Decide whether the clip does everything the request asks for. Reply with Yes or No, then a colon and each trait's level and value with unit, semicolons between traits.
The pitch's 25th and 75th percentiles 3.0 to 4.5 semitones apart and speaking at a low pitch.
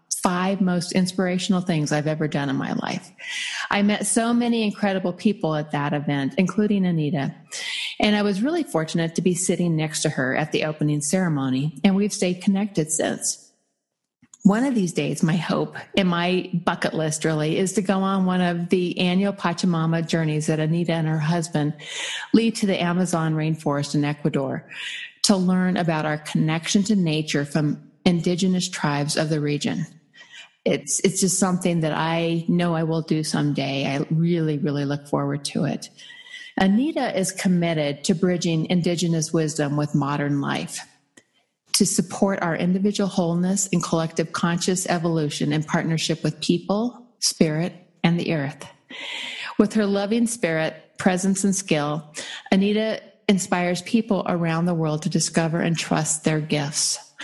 No: average, 4.0 semitones; medium, 175 Hz